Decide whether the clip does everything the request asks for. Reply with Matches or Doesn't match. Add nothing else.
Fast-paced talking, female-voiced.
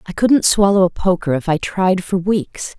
Matches